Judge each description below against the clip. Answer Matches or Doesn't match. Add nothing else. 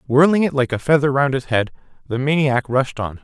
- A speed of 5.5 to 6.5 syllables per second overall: Matches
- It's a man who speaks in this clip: Matches